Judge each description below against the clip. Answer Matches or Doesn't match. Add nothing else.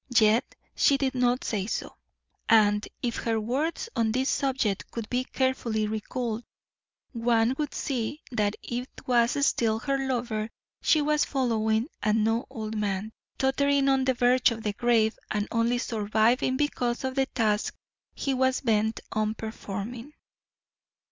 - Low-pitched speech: Doesn't match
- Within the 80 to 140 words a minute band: Doesn't match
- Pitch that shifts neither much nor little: Matches